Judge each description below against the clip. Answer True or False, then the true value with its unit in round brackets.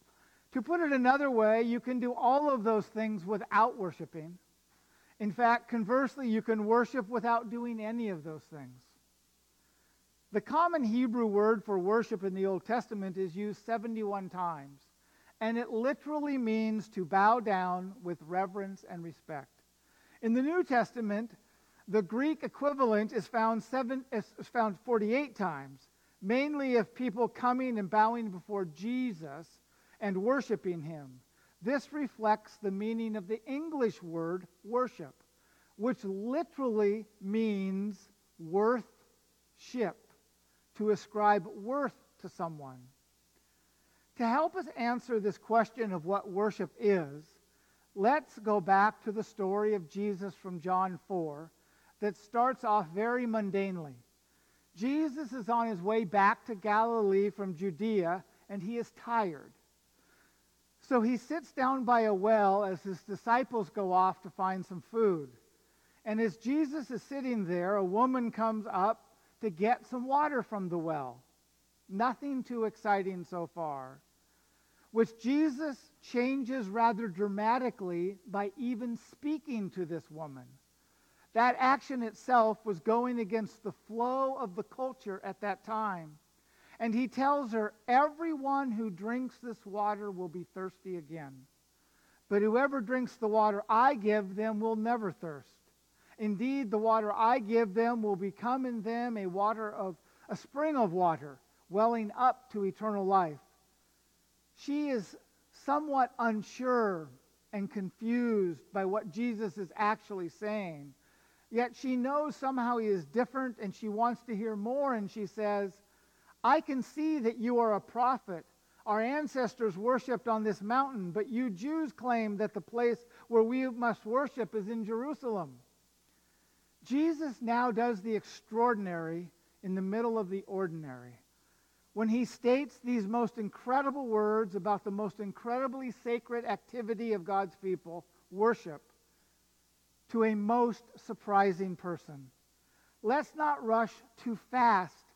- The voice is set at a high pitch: True (215 Hz)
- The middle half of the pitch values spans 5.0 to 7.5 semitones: False (4.0 semitones)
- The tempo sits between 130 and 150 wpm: True (140 wpm)